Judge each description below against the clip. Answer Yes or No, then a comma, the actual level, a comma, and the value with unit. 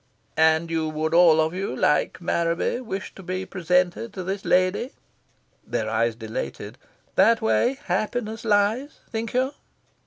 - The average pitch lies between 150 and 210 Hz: Yes, medium, 185 Hz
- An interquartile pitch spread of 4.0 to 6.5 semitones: Yes, wide, 5.5 semitones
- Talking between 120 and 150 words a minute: Yes, average, 145 wpm